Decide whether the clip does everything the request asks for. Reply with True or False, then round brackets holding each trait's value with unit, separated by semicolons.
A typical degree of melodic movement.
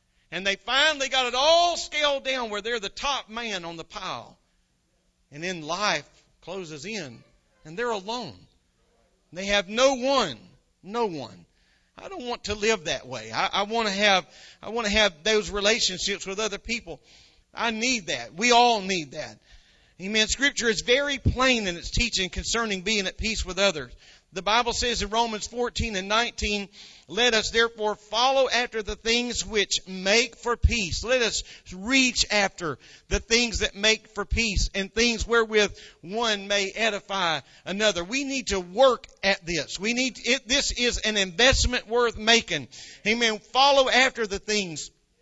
True (3.7 semitones)